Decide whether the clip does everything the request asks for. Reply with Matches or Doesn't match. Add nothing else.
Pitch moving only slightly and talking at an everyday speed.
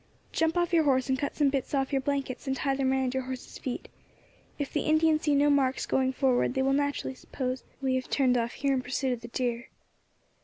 Doesn't match